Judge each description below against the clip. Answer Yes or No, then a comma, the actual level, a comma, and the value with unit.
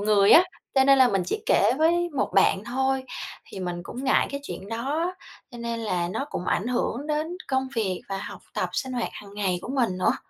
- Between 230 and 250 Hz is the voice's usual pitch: Yes, high, 240 Hz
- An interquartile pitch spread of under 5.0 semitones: No, average, 5.3 semitones